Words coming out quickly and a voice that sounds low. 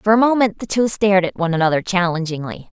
No: fast, 215 wpm; high, 190 Hz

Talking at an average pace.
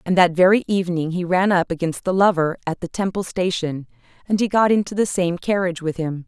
No: fast, 220 wpm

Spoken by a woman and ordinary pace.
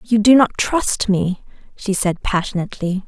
Yes: female; average, 155 wpm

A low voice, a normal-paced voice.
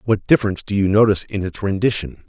No: low, 100 Hz; fast, 210 wpm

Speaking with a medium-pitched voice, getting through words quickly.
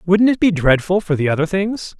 Yes: medium, 180 Hz; fast, 240 wpm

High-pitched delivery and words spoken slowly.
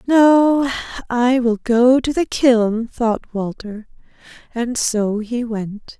Yes: high, 240 Hz; slow, 130 wpm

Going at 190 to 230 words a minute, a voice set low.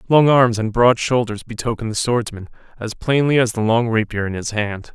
Yes: fast, 205 wpm; low, 115 Hz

